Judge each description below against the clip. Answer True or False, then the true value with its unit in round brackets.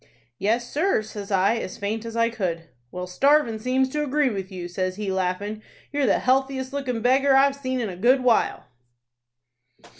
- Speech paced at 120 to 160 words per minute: False (180 wpm)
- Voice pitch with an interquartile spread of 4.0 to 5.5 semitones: True (5.2 semitones)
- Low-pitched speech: False (230 Hz)